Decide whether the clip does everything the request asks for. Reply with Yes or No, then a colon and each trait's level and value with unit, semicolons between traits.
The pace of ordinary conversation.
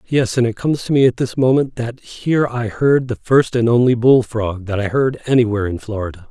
No: fast, 240 wpm